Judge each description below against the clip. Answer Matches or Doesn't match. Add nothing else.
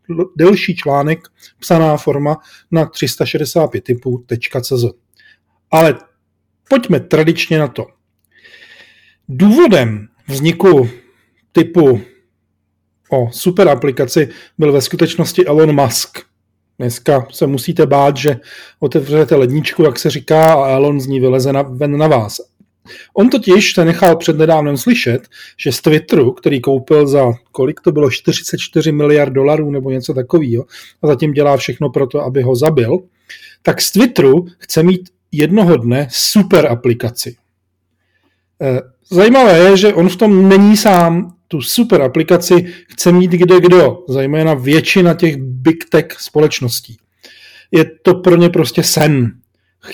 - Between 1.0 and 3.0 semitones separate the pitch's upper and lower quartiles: Doesn't match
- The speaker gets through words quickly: Doesn't match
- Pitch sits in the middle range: Matches